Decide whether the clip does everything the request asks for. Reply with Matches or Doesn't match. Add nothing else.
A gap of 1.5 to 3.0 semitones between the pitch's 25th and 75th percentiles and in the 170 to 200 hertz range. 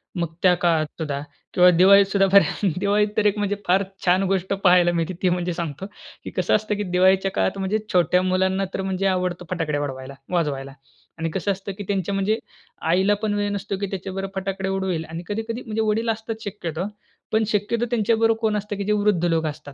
Matches